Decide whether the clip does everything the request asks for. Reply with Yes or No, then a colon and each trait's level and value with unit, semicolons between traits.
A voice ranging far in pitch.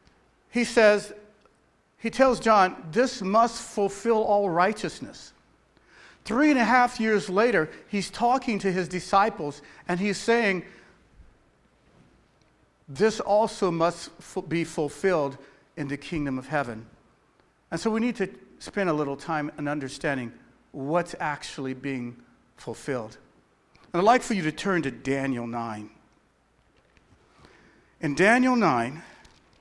Yes: wide, 7.1 semitones